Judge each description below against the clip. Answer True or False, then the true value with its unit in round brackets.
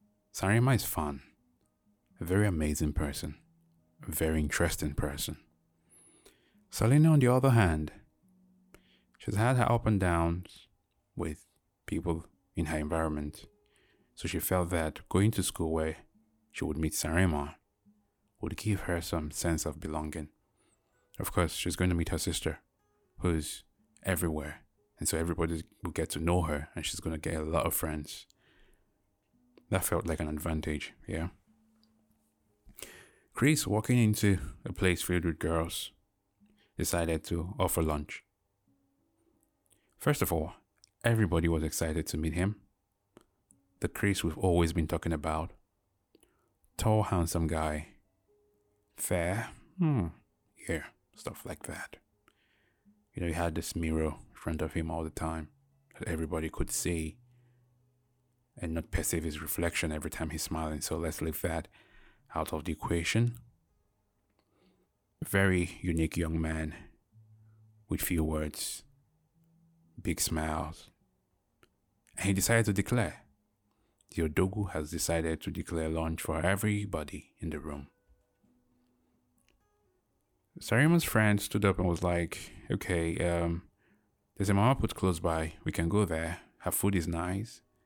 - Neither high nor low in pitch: False (90 Hz)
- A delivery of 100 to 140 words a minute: True (135 wpm)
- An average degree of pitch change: True (4.3 semitones)